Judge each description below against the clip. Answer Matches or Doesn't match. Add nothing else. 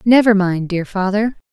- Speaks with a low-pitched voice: Doesn't match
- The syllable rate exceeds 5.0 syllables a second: Doesn't match